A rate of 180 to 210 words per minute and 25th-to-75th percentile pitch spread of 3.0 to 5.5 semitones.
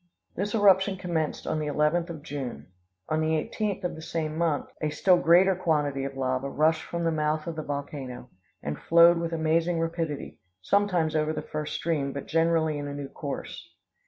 No: average, 190 wpm; narrow, 2.5 semitones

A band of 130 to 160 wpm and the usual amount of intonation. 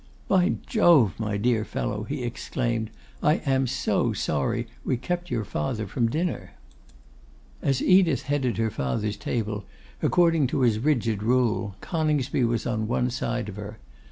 Yes: average, 150 wpm; average, 4.6 semitones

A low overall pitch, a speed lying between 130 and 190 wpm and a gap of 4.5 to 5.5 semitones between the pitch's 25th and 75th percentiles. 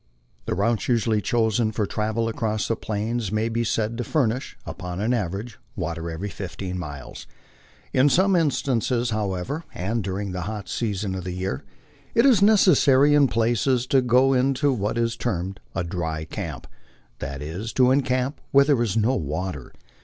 Yes: low, 110 Hz; average, 170 wpm; average, 5.1 semitones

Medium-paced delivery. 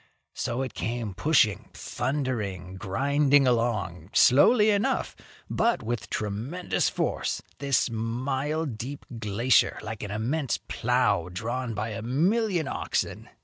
No: slow, 115 wpm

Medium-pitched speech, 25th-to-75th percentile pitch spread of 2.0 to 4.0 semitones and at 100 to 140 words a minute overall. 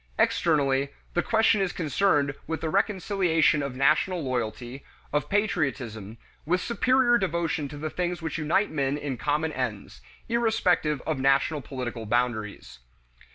No: medium, 150 Hz; average, 5.2 semitones; slow, 135 wpm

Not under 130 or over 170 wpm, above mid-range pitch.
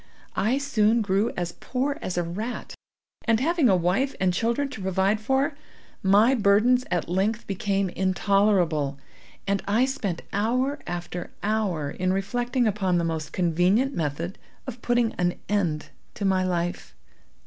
Yes: average, 150 wpm; high, 200 Hz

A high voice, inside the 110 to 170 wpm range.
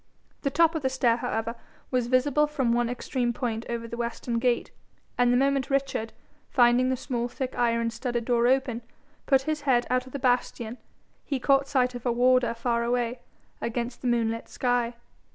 No: high, 245 Hz; average, 185 wpm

